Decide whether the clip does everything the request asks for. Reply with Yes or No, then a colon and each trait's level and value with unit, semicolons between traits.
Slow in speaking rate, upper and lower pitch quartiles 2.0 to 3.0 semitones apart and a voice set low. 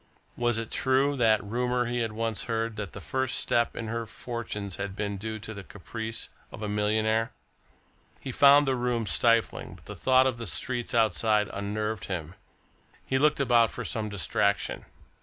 No: average, 175 wpm; average, 2.7 semitones; low, 115 Hz